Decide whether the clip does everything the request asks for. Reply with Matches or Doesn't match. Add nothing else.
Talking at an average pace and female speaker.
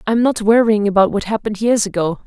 Doesn't match